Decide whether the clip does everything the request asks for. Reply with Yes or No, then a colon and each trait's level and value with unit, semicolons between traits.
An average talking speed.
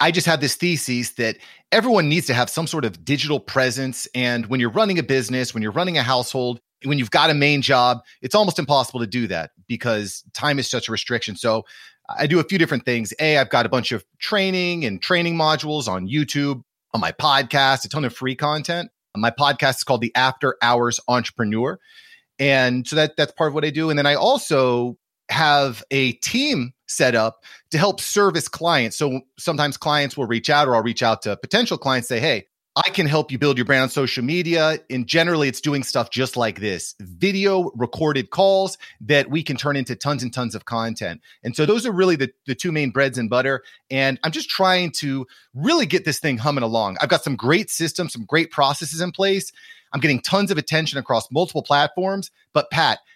No: fast, 215 wpm